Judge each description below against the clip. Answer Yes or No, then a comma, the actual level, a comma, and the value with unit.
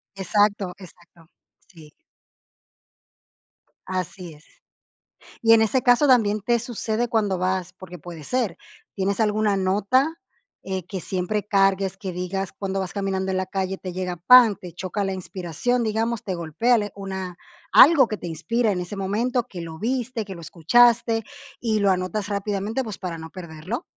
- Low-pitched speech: No, high, 195 Hz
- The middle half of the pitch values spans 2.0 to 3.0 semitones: No, average, 3.4 semitones